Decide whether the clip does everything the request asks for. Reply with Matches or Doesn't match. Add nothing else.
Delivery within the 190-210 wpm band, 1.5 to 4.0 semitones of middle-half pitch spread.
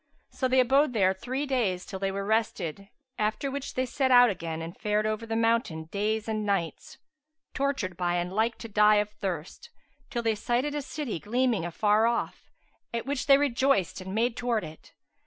Doesn't match